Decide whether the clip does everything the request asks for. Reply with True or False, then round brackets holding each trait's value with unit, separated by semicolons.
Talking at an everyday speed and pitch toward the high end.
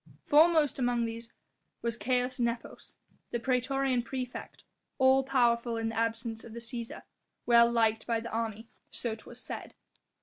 True (145 wpm; 235 Hz)